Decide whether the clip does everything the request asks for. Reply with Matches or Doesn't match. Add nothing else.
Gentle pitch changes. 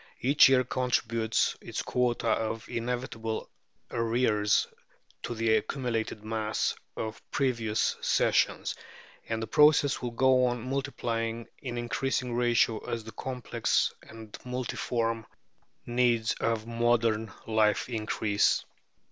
Matches